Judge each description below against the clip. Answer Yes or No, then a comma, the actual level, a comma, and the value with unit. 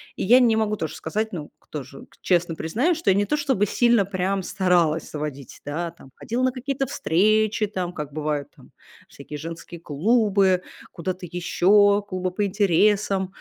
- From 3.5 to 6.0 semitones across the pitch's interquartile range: Yes, average, 4.6 semitones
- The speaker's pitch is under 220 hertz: Yes, high, 190 Hz